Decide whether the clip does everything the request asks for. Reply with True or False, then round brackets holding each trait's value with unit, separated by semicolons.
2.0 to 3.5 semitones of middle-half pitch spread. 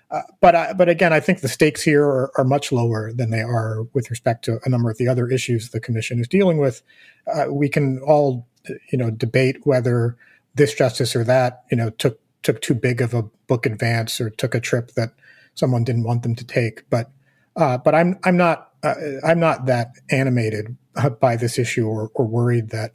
True (2.9 semitones)